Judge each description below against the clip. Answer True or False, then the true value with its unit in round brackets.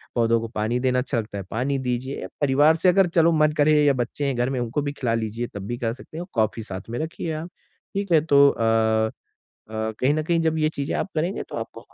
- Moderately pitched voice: False (130 Hz)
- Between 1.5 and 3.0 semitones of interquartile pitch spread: False (5.3 semitones)